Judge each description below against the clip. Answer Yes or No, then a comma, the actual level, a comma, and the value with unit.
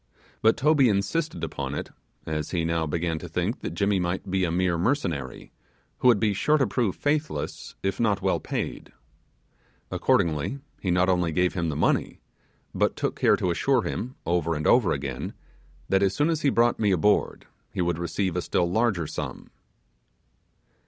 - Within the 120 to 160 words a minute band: No, average, 180 wpm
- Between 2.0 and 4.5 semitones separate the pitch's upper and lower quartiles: No, average, 5.3 semitones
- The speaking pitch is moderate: No, very low, 95 Hz